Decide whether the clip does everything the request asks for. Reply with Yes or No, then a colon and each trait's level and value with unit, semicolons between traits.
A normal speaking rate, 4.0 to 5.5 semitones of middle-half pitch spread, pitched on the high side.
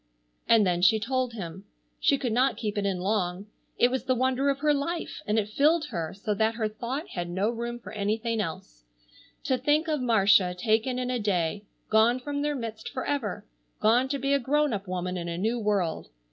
No: fast, 210 wpm; average, 4.6 semitones; high, 225 Hz